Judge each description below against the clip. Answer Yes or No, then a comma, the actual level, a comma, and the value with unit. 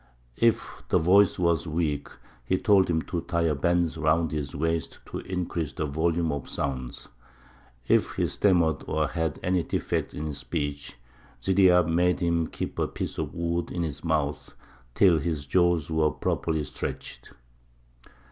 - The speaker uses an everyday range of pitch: No, narrow, 2.3 semitones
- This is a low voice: Yes, very low, 80 Hz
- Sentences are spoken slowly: No, average, 155 wpm